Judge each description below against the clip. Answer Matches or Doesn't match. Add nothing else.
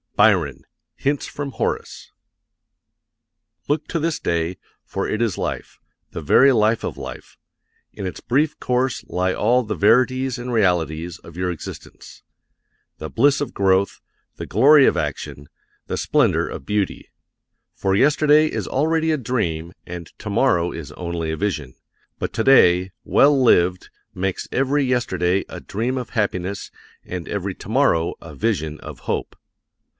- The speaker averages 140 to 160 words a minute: Matches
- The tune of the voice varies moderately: Doesn't match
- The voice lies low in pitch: Matches